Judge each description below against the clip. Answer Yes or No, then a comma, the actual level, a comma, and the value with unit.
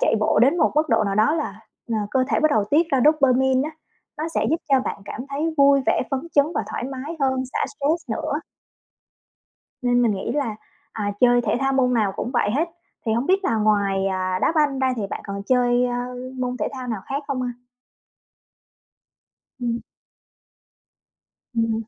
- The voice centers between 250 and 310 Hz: Yes, very high, 255 Hz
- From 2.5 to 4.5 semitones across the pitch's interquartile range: Yes, average, 3.7 semitones